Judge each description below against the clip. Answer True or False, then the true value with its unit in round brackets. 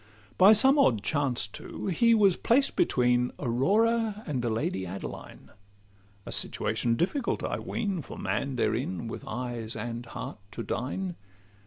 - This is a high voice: False (135 Hz)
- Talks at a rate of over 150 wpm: False (145 wpm)